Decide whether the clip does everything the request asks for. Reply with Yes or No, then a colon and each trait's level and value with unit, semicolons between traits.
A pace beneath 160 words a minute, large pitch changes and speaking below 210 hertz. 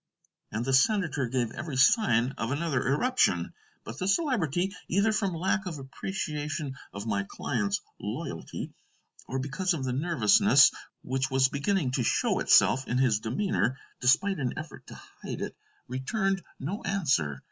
Yes: average, 150 wpm; wide, 6.9 semitones; medium, 140 Hz